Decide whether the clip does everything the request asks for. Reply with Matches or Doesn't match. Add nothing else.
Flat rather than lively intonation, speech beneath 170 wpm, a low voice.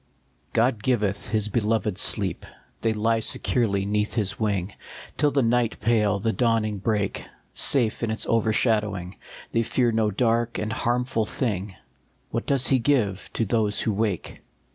Matches